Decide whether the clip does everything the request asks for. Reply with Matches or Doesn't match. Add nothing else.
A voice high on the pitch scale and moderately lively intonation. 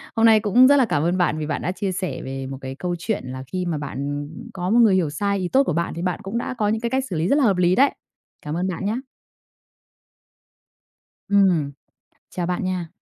Doesn't match